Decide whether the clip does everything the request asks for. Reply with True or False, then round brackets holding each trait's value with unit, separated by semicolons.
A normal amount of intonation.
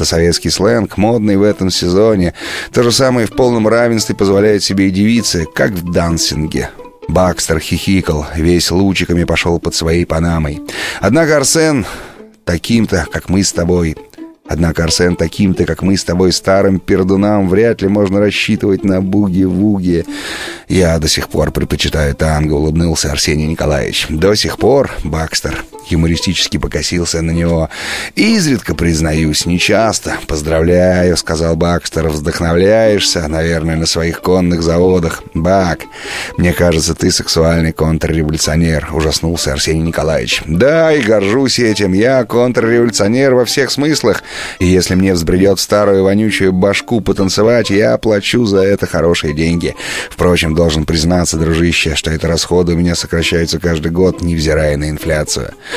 True (3.4 semitones)